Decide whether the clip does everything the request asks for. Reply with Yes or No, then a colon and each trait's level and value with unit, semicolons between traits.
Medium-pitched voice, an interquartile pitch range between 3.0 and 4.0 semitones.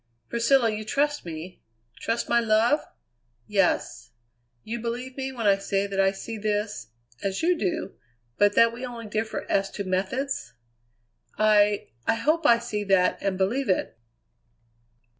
No: high, 215 Hz; average, 3.3 semitones